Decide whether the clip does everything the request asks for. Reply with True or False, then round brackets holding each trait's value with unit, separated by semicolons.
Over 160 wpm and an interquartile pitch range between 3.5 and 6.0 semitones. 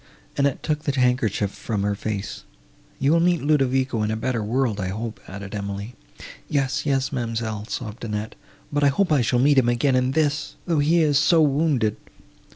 True (170 wpm; 4.9 semitones)